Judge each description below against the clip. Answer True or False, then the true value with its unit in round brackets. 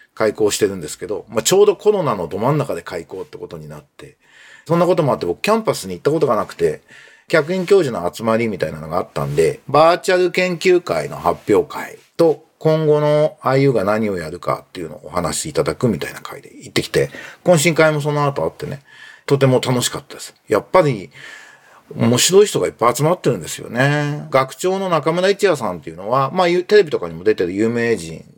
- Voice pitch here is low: False (165 Hz)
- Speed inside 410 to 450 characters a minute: True (425 characters per minute)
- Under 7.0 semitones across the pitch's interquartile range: False (7.4 semitones)